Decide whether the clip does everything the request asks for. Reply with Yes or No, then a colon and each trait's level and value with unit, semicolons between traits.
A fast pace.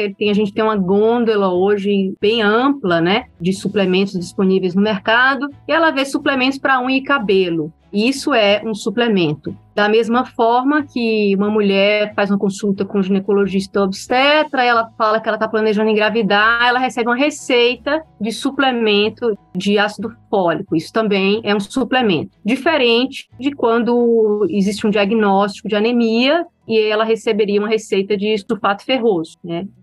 No: average, 155 wpm